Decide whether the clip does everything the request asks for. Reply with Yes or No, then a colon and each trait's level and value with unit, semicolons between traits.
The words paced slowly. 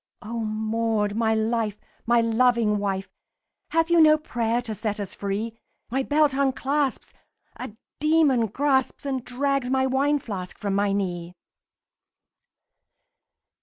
Yes: slow, 130 wpm